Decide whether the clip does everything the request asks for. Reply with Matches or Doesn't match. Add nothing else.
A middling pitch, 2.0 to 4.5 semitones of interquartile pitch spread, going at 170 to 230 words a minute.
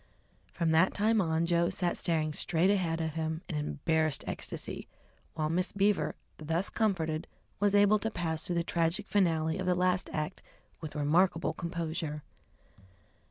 Doesn't match